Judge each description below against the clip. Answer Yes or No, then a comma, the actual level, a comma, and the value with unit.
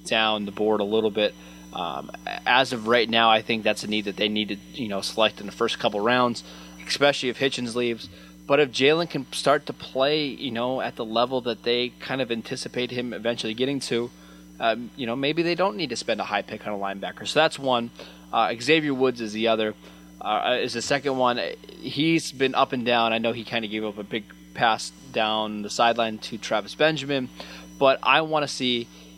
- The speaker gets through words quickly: Yes, fast, 220 wpm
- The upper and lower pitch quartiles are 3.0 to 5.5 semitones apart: Yes, average, 3.8 semitones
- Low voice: Yes, low, 115 Hz